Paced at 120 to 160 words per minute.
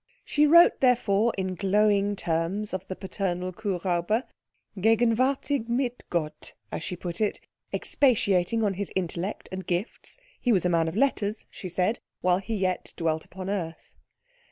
Yes: average, 155 wpm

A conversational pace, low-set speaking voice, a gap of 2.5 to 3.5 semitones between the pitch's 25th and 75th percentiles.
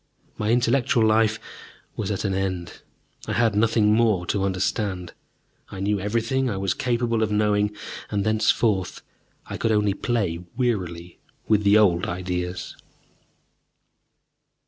No: slow, 130 wpm; low, 105 Hz; average, 2.8 semitones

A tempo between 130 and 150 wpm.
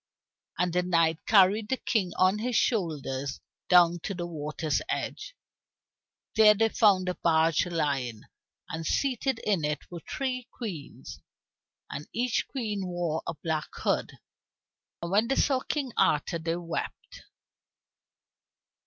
Yes: slow, 135 wpm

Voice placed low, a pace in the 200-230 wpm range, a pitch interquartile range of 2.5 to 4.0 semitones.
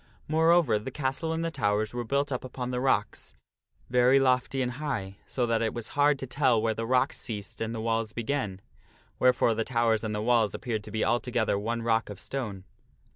Yes: low, 120 Hz; fast, 205 wpm; average, 3.1 semitones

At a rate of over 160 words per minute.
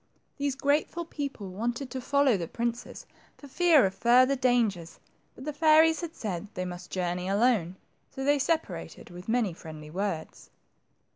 No: average, 155 wpm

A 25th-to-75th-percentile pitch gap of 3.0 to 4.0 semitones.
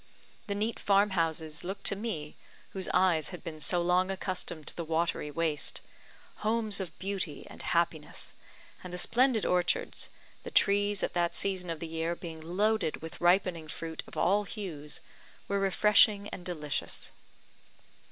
Yes: average, 3.5 semitones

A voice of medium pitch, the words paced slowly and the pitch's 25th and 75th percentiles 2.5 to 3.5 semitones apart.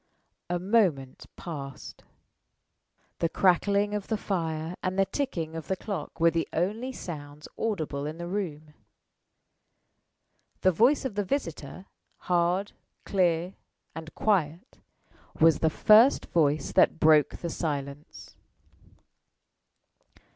No: medium, 170 Hz; slow, 115 wpm; average, 4.2 semitones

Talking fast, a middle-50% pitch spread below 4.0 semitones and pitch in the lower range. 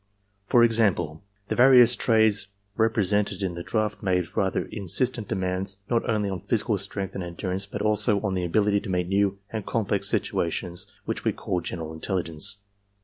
No: average, 165 wpm; average, 2.9 semitones; low, 100 Hz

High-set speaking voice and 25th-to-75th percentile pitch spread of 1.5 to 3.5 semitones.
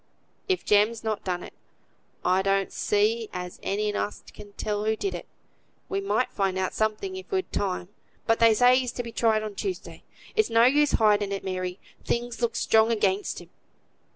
Yes: high, 215 Hz; average, 3.2 semitones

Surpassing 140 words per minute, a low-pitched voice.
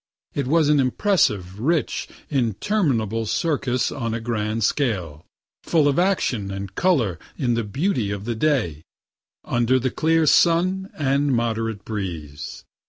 No: slow, 135 wpm; low, 120 Hz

